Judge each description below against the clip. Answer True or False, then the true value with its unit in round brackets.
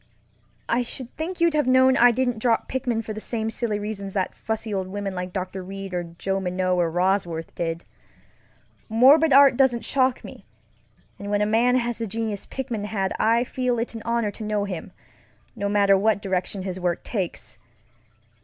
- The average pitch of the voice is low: False (215 Hz)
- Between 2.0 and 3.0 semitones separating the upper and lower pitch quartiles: False (4.0 semitones)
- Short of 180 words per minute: False (185 wpm)